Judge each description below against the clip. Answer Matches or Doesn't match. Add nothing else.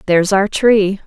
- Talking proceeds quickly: Doesn't match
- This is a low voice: Doesn't match